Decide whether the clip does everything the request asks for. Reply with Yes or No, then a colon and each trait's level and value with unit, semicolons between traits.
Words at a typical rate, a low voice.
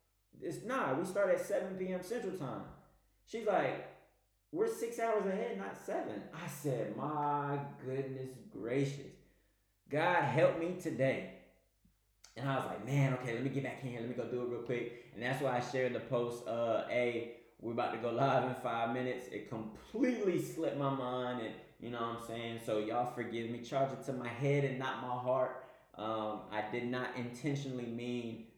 Yes: average, 195 wpm; low, 125 Hz